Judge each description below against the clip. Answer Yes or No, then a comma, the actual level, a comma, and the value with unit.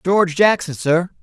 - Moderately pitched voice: Yes, medium, 175 Hz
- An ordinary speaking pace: Yes, average, 145 wpm